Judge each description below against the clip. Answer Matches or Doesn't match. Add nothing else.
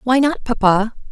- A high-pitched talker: Matches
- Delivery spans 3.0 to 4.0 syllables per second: Doesn't match